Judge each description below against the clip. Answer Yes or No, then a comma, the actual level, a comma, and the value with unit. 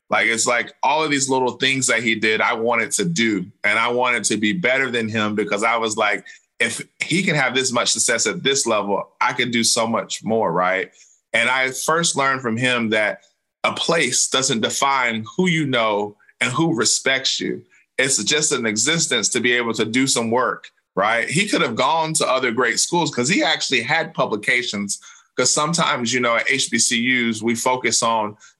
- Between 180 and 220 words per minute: Yes, average, 200 wpm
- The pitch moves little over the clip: No, average, 3.0 semitones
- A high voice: No, low, 120 Hz